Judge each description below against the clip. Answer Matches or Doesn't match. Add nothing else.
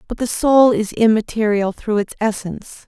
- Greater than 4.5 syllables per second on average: Matches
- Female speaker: Matches